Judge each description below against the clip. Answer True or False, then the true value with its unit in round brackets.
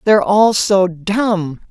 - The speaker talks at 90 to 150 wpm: True (140 wpm)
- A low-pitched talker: False (195 Hz)